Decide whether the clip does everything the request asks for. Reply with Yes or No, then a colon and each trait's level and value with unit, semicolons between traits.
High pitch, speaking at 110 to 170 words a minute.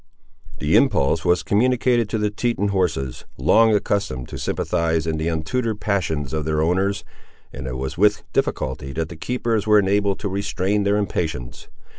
No: very low, 95 Hz; average, 165 wpm